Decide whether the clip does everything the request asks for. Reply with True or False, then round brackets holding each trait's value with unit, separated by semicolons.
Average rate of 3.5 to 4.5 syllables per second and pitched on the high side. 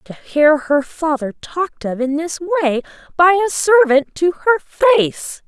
True (4.1 syllables/s; 320 Hz)